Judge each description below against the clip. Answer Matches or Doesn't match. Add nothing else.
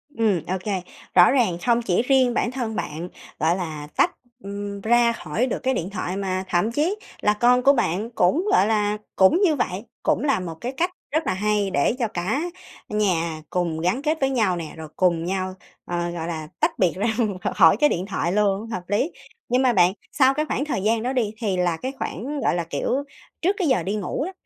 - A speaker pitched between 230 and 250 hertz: Doesn't match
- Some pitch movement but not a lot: Doesn't match